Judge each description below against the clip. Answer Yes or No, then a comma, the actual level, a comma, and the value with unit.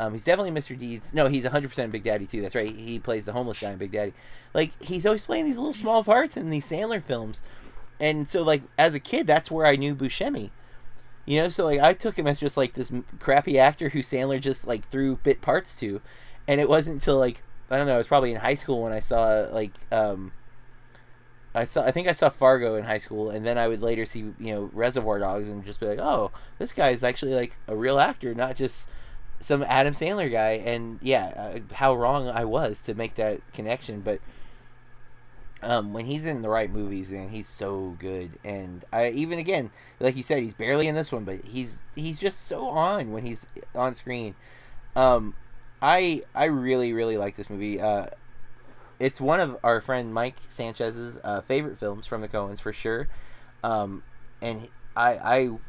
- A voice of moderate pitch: No, low, 125 Hz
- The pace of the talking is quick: Yes, fast, 210 wpm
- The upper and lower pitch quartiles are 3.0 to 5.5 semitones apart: Yes, average, 3.6 semitones